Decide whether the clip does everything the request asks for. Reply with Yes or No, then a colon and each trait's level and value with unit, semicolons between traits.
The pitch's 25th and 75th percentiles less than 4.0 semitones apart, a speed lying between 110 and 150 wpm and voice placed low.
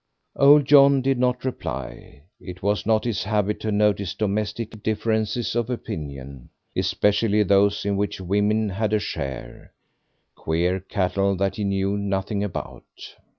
Yes: narrow, 2.4 semitones; average, 140 wpm; low, 100 Hz